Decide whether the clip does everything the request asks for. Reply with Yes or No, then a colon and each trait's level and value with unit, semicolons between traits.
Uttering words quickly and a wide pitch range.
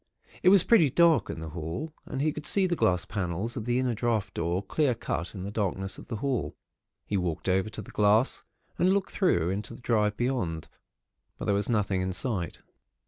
Yes: fast, 210 wpm; wide, 5.9 semitones